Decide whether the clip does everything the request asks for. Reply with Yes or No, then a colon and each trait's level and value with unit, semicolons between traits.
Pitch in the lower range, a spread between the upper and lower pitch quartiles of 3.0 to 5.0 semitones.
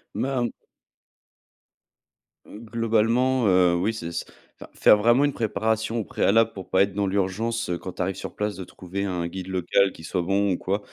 Yes: low, 100 Hz; average, 3.4 semitones